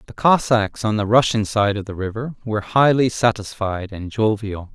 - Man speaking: Yes, male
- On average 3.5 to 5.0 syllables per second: Yes, 4.9 syllables/s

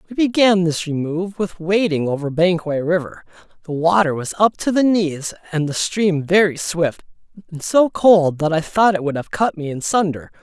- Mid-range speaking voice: Yes, medium, 175 Hz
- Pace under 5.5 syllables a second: Yes, 4.9 syllables/s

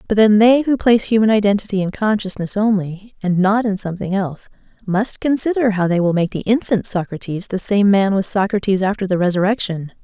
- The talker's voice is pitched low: No, high, 200 Hz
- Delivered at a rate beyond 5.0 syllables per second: Yes, 5.8 syllables/s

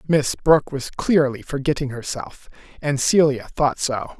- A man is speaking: Yes, male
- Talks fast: No, average, 145 wpm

